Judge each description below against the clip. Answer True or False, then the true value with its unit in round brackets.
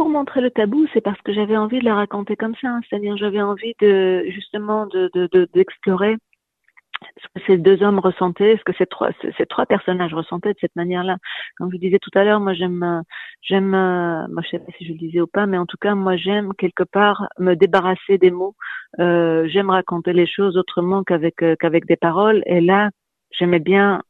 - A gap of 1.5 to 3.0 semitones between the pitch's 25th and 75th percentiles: True (2.6 semitones)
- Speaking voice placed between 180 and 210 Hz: True (190 Hz)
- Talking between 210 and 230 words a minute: True (220 wpm)